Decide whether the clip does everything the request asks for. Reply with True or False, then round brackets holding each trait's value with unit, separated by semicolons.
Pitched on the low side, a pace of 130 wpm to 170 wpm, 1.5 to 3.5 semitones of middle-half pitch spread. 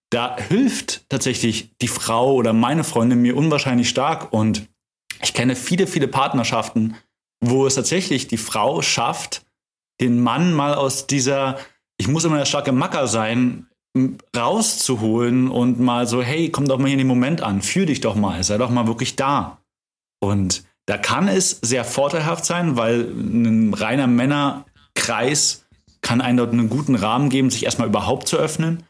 True (125 Hz; 165 wpm; 3.2 semitones)